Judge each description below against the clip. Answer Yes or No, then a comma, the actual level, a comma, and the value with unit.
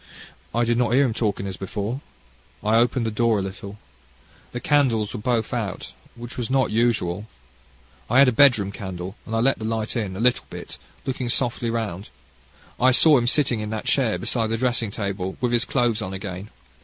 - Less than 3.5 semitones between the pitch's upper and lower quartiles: Yes, average, 2.9 semitones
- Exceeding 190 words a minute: Yes, average, 200 wpm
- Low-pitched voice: Yes, low, 115 Hz